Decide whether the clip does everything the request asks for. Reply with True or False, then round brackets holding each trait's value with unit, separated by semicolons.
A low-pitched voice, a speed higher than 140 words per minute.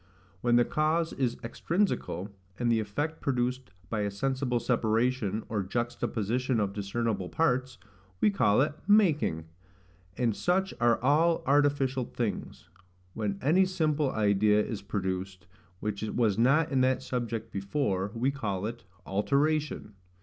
False (120 Hz; 135 wpm)